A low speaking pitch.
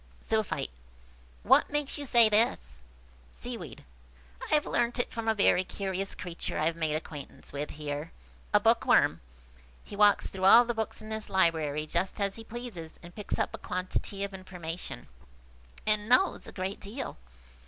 No: high, 190 Hz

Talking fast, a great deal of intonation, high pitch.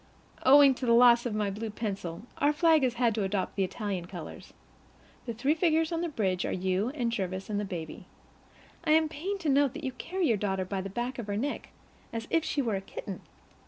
Yes: fast, 230 wpm; wide, 6.8 semitones; high, 230 Hz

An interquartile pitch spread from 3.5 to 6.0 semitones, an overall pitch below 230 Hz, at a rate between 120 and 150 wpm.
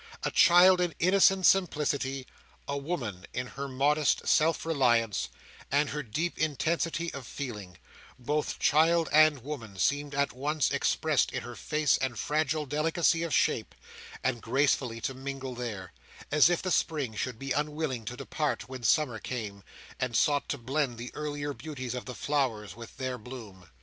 No: average, 3.8 semitones; medium, 140 Hz; average, 160 wpm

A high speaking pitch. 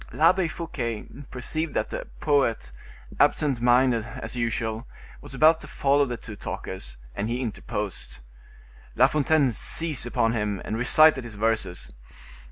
No: low, 120 Hz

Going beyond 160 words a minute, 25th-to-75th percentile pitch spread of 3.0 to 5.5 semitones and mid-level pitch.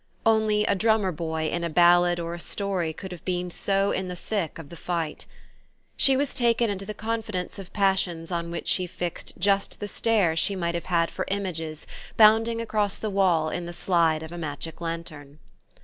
Yes: average, 195 wpm; average, 3.3 semitones; medium, 180 Hz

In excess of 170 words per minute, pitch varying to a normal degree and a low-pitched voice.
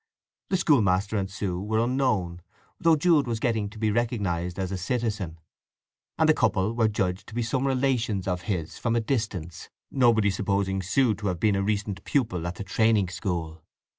Yes: average, 185 wpm; average, 4.0 semitones; low, 105 Hz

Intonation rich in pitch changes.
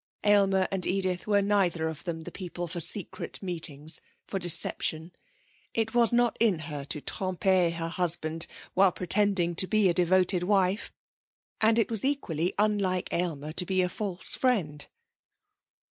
No: average, 3.1 semitones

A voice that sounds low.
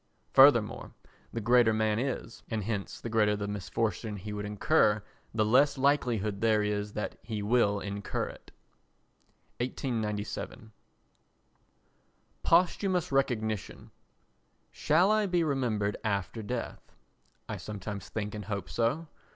Yes: low, 110 Hz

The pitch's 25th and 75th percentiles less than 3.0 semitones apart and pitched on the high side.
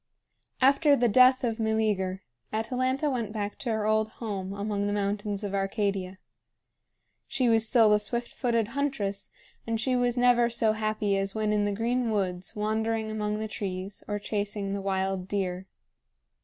Yes: narrow, 2.6 semitones; high, 215 Hz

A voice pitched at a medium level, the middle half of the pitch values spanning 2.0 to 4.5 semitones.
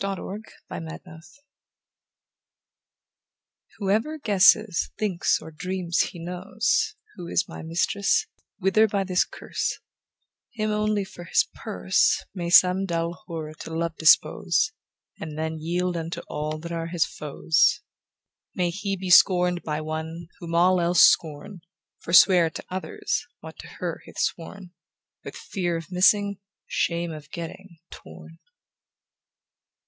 Yes: medium, 175 Hz; average, 2.9 semitones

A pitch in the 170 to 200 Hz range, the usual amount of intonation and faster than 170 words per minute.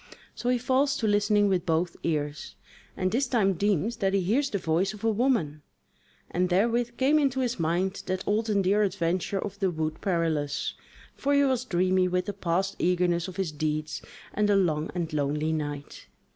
Yes: high, 190 Hz; average, 4.6 semitones; average, 190 wpm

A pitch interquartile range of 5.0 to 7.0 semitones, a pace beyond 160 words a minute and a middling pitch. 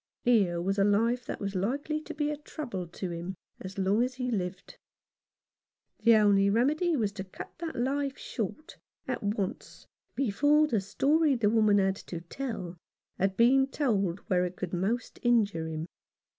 No: wide, 5.6 semitones; average, 170 wpm; high, 215 Hz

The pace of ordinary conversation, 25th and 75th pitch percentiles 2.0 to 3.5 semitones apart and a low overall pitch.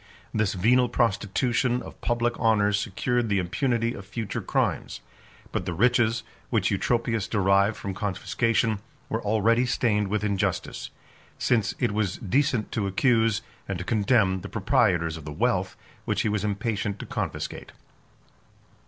Yes: average, 145 wpm; average, 3.1 semitones; low, 110 Hz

